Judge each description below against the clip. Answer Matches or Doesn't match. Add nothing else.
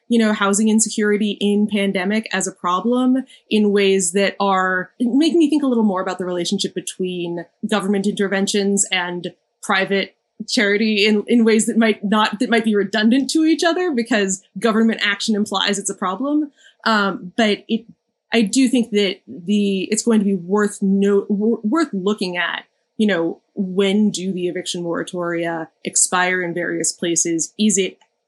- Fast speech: Doesn't match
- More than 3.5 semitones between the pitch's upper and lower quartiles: Doesn't match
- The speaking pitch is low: Doesn't match